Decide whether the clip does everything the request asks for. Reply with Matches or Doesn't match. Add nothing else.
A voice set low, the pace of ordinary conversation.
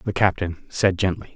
Matches